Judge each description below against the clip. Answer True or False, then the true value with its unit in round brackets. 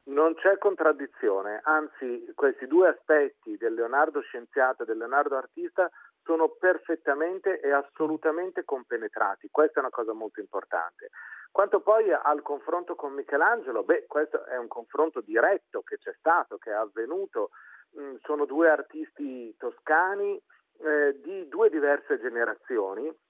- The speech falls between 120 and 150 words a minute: True (130 wpm)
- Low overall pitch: False (220 Hz)